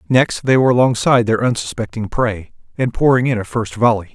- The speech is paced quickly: No, average, 190 wpm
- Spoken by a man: Yes, male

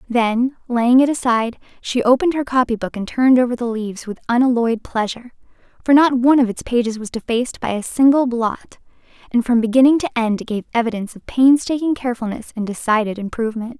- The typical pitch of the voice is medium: No, high, 240 Hz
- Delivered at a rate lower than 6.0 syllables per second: No, 6.3 syllables/s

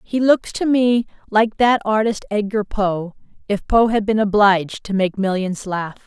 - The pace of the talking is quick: No, average, 180 wpm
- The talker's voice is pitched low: No, high, 210 Hz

